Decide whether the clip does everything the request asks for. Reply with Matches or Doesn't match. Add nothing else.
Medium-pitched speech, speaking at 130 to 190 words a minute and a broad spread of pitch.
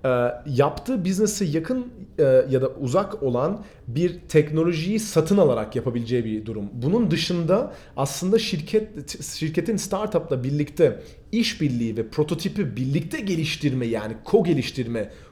Doesn't match